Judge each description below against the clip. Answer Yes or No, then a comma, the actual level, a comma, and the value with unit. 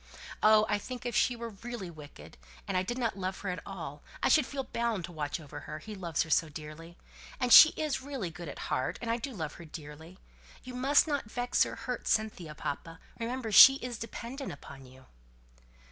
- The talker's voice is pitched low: No, high, 200 Hz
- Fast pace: Yes, fast, 210 wpm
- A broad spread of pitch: Yes, wide, 7.3 semitones